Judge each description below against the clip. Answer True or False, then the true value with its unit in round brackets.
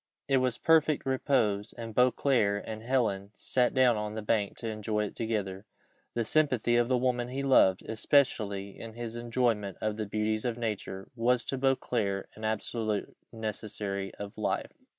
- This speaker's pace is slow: False (165 wpm)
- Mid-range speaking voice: False (115 Hz)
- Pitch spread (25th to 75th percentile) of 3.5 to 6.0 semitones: False (3.1 semitones)